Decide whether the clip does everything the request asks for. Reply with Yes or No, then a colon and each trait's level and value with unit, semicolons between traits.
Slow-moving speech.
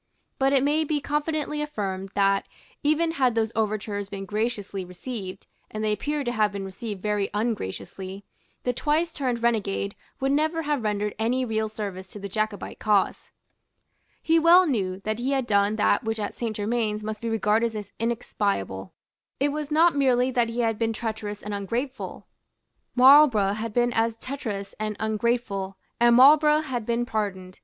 No: average, 170 wpm